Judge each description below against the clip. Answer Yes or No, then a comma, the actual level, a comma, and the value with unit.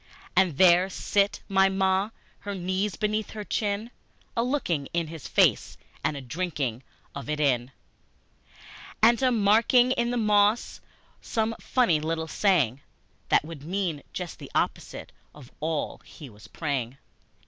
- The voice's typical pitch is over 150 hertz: Yes, medium, 185 Hz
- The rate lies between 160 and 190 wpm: No, average, 145 wpm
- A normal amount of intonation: No, wide, 5.7 semitones